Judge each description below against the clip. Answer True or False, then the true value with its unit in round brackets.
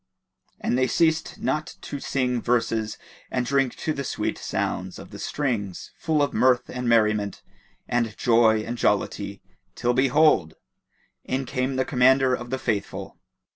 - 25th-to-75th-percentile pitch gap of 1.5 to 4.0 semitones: True (2.8 semitones)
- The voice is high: False (125 Hz)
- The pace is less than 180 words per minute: True (150 wpm)